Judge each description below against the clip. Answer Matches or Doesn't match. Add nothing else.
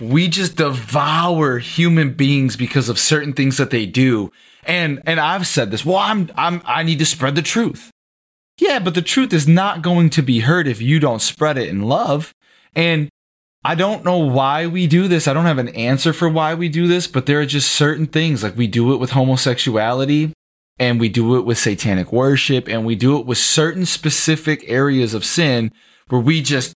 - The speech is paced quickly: Matches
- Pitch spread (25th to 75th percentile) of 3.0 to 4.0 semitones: Doesn't match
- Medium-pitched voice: Matches